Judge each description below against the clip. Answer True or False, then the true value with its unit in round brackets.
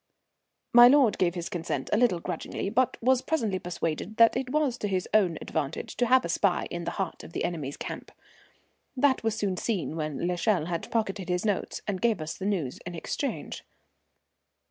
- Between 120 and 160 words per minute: False (190 wpm)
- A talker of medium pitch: False (195 Hz)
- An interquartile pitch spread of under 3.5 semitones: False (5.2 semitones)